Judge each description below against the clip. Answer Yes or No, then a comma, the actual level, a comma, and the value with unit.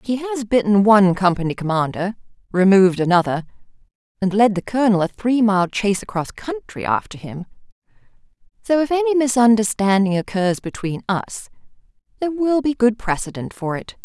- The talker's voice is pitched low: No, high, 210 Hz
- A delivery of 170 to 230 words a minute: No, average, 145 wpm